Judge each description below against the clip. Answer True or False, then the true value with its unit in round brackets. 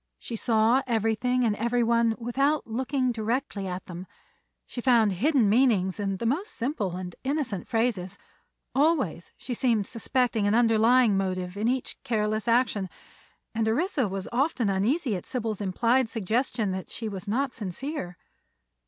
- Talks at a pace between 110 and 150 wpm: True (145 wpm)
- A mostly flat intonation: False (3.9 semitones)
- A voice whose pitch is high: True (230 Hz)